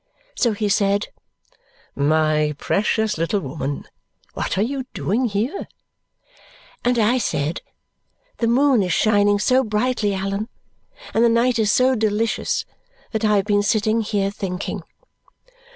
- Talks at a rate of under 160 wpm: Yes, slow, 135 wpm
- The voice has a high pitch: Yes, high, 210 Hz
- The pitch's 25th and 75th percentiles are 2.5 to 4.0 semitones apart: Yes, average, 2.8 semitones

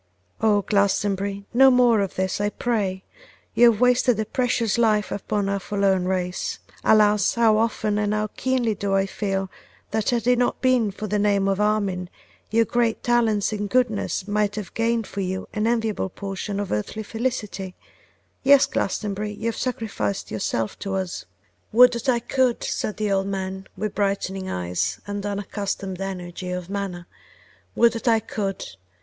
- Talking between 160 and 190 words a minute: Yes, average, 170 wpm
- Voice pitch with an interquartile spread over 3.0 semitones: No, average, 2.7 semitones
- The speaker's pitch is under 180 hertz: No, high, 205 Hz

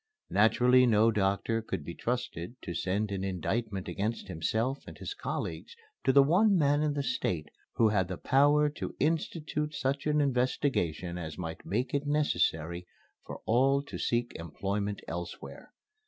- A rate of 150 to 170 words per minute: Yes, average, 155 wpm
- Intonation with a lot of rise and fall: Yes, wide, 7.1 semitones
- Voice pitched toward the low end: Yes, low, 115 Hz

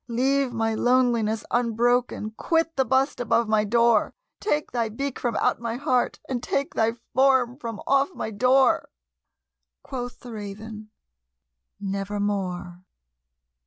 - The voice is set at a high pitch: Yes, high, 235 Hz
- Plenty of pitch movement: No, average, 3.1 semitones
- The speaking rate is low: Yes, slow, 125 wpm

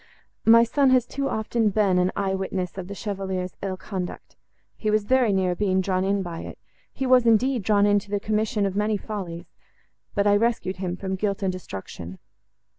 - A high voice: Yes, high, 200 Hz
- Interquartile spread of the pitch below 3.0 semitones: Yes, narrow, 2.6 semitones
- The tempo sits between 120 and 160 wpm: No, average, 195 wpm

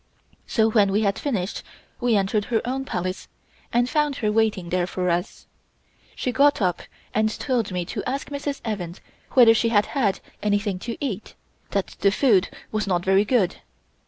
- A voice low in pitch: No, high, 210 Hz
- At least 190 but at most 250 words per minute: No, average, 175 wpm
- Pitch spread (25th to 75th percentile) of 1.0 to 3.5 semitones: No, average, 4.2 semitones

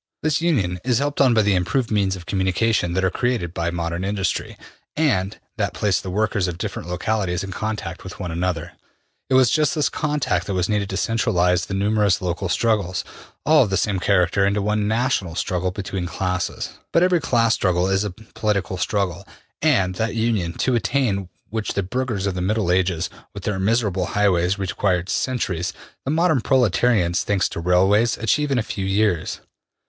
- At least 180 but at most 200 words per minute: Yes, average, 185 wpm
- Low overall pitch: Yes, low, 100 Hz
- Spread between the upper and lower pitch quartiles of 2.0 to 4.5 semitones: Yes, average, 3.8 semitones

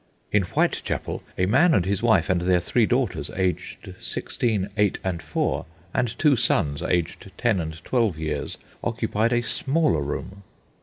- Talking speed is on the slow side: No, average, 155 wpm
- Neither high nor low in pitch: No, low, 100 Hz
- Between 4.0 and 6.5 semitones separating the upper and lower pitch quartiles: Yes, wide, 5.4 semitones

